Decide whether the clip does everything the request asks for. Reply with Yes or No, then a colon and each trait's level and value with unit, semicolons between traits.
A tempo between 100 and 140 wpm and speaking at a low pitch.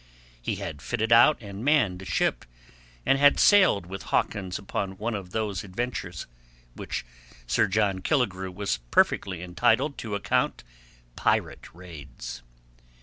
Yes: slow, 135 wpm; low, 100 Hz